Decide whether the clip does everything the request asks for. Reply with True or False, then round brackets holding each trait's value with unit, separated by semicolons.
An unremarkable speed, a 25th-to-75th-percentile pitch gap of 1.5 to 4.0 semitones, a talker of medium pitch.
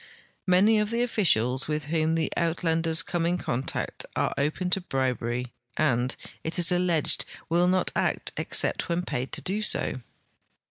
False (155 wpm; 4.6 semitones; 165 Hz)